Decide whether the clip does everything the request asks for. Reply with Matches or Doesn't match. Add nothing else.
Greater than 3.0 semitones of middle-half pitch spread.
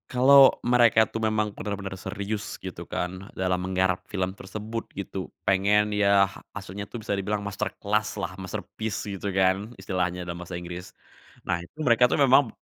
Doesn't match